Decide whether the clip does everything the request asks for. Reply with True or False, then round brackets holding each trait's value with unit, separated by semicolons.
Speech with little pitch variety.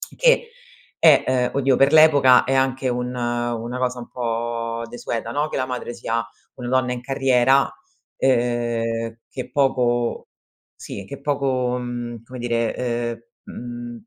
True (1.8 semitones)